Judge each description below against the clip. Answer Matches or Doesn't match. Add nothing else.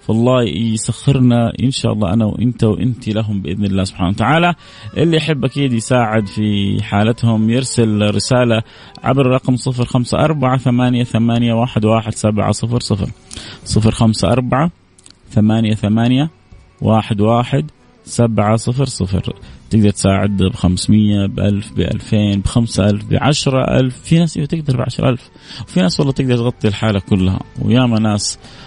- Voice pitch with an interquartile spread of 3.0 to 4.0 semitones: Matches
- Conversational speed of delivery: Doesn't match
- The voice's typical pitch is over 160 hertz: Doesn't match